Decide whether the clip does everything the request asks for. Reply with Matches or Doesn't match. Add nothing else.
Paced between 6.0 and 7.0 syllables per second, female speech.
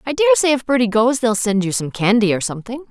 Matches